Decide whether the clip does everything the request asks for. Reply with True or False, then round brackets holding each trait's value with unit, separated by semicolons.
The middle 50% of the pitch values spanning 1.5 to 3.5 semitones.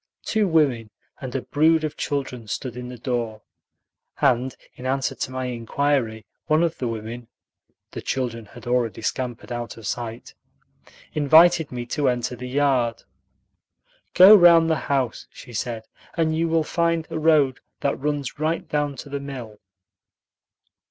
False (4.3 semitones)